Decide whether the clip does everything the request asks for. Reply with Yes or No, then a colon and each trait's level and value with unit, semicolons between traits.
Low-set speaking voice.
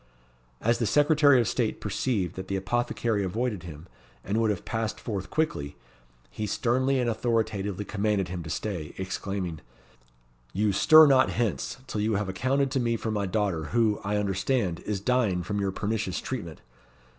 Yes: low, 105 Hz